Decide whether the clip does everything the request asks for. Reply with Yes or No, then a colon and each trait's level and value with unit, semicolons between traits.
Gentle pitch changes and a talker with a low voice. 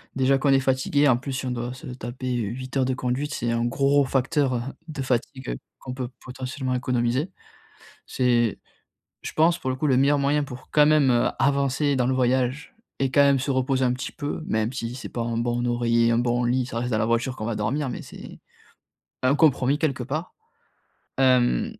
Yes: narrow, 2.3 semitones; low, 130 Hz